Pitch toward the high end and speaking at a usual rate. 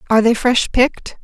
Yes: high, 235 Hz; average, 195 wpm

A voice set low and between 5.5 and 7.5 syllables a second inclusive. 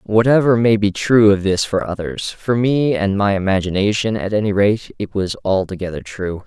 No: low, 105 Hz; 4.9 syllables/s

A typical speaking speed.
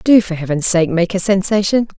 No: fast, 210 wpm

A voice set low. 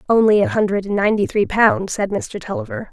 No: high, 210 Hz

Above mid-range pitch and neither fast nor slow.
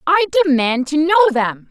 Yes: very high, 290 Hz; average, 175 wpm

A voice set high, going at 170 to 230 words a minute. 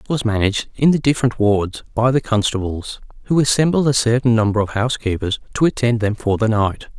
No: low, 115 Hz; average, 200 wpm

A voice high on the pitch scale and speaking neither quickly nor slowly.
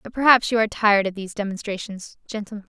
Yes: high, 210 Hz; average, 195 wpm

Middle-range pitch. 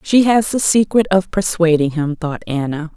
Yes: medium, 180 Hz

